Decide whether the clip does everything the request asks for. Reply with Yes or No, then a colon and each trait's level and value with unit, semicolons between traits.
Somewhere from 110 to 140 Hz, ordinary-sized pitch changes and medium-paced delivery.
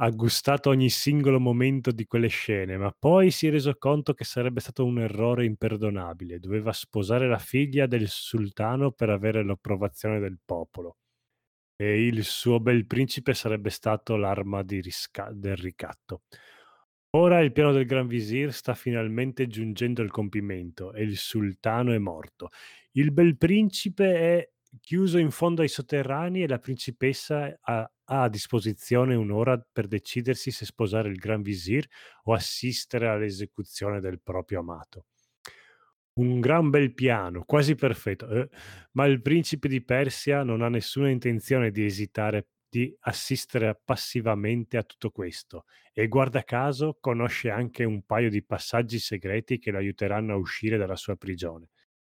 Yes: low, 115 Hz; average, 4.1 semitones; average, 150 wpm